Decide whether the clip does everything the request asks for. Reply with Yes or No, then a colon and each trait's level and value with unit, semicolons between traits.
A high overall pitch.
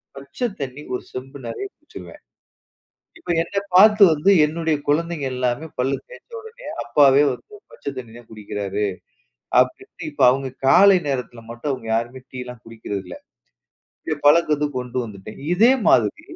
No: low, 135 Hz